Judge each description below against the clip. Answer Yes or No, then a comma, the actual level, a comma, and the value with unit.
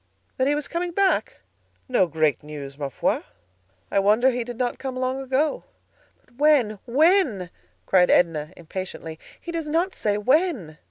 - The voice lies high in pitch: Yes, high, 245 Hz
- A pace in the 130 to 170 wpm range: Yes, average, 160 wpm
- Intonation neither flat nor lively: No, wide, 9.0 semitones